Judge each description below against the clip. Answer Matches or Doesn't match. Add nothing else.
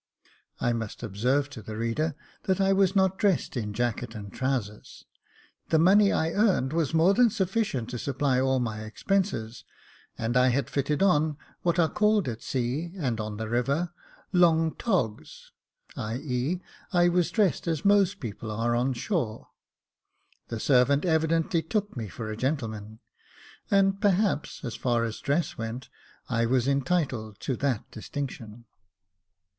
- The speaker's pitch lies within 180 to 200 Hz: Doesn't match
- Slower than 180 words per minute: Matches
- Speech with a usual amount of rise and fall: Doesn't match